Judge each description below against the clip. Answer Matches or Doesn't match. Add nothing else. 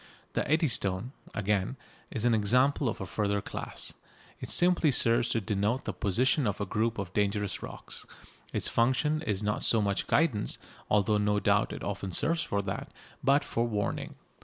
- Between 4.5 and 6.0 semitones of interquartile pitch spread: Doesn't match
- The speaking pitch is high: Doesn't match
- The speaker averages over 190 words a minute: Doesn't match